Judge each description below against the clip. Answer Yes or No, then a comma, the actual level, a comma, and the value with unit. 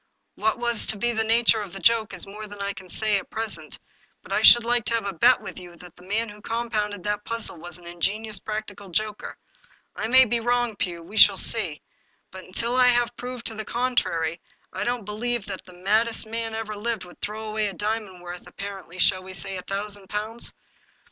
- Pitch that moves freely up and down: No, average, 3.2 semitones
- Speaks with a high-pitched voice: Yes, high, 210 Hz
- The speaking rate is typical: No, fast, 220 wpm